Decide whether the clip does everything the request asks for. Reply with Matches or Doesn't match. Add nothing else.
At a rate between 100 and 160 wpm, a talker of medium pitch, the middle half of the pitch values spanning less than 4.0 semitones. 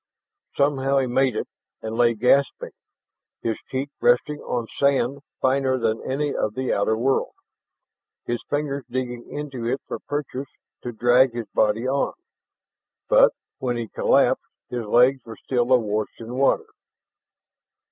Doesn't match